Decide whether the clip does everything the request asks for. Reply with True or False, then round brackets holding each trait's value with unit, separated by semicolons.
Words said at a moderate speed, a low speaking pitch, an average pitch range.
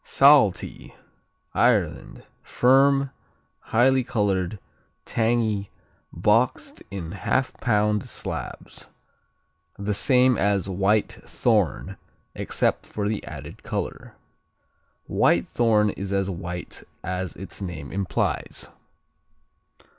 False (85 wpm; 105 Hz; 3.7 semitones)